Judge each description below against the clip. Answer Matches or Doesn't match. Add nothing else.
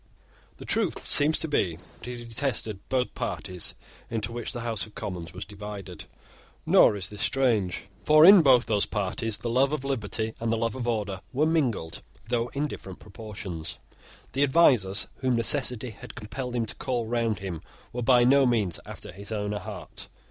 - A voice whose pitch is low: Matches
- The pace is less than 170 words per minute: Doesn't match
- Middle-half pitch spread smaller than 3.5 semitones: Doesn't match